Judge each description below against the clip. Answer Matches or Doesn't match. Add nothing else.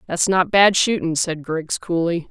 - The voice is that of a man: Doesn't match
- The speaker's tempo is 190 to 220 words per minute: Doesn't match